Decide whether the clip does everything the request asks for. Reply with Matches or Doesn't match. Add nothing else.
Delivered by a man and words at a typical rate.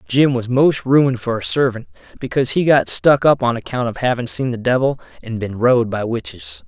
Doesn't match